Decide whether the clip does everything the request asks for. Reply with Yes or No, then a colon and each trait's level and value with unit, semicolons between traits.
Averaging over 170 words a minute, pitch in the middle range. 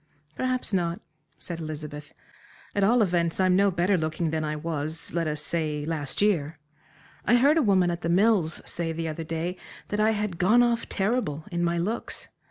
Yes: average, 185 wpm; medium, 170 Hz